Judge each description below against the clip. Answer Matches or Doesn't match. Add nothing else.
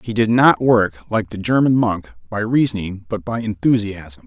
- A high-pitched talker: Doesn't match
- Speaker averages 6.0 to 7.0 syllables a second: Doesn't match